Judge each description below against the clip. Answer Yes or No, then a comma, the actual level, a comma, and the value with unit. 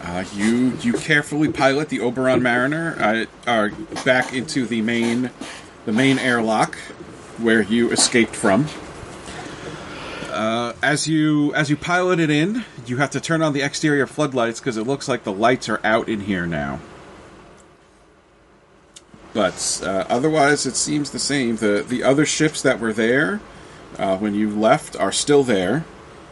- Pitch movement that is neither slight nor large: Yes, average, 4.4 semitones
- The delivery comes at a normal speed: Yes, average, 155 wpm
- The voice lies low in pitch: Yes, low, 130 Hz